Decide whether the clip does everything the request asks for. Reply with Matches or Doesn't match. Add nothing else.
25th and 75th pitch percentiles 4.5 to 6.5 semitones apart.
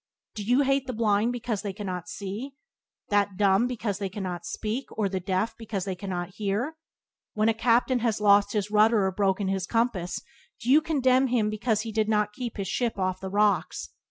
Doesn't match